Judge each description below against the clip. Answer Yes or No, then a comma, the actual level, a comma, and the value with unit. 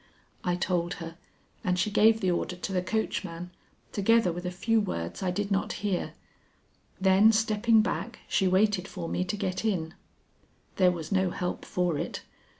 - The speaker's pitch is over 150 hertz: Yes, medium, 185 Hz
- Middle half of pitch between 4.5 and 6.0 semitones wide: No, average, 2.7 semitones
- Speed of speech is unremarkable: Yes, average, 170 wpm